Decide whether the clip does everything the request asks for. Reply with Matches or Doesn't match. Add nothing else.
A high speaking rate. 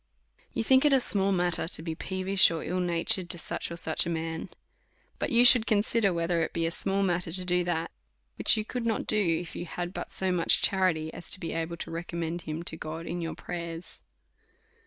Matches